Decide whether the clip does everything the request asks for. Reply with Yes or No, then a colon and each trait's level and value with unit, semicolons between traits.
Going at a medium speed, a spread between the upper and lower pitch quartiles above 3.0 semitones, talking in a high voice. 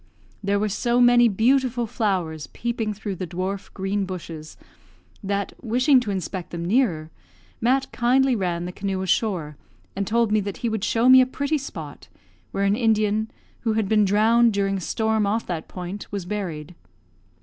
Yes: average, 170 wpm; average, 3.8 semitones; high, 205 Hz